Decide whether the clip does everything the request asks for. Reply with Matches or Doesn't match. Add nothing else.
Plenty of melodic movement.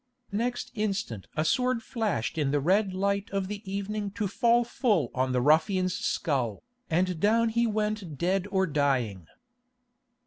Matches